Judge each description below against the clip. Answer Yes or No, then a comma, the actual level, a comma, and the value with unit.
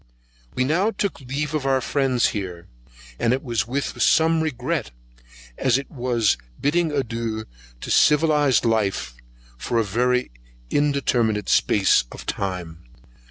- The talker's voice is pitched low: Yes, low, 125 Hz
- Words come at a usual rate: No, slow, 130 wpm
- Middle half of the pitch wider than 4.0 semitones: Yes, average, 4.5 semitones